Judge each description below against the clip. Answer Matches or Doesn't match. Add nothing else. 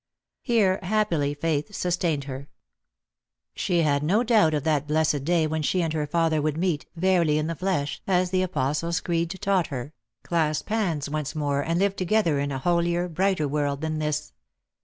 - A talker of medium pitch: Matches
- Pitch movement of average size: Matches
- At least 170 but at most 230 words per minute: Matches